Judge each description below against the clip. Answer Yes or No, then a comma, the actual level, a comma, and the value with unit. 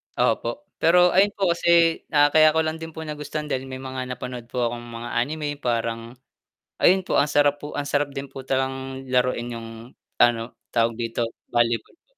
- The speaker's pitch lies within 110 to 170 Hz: Yes, low, 135 Hz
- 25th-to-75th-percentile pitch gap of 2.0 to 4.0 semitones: No, average, 4.4 semitones